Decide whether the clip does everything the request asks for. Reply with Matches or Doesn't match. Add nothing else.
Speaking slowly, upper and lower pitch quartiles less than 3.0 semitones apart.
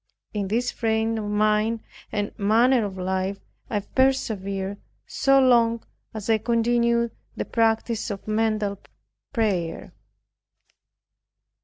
Matches